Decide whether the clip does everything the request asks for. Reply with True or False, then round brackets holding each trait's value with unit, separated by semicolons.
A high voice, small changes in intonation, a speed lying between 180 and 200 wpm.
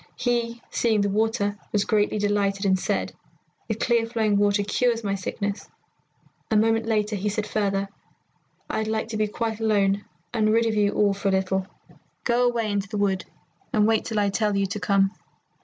True (210 Hz; 2.0 semitones; 190 wpm)